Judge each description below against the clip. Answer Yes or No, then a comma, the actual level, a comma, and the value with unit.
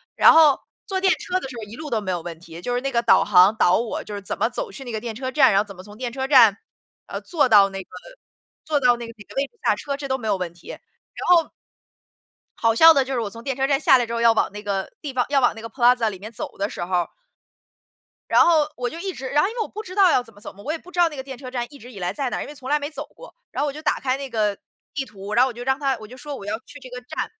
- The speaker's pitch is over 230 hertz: Yes, very high, 250 Hz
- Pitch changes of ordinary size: Yes, average, 5.0 semitones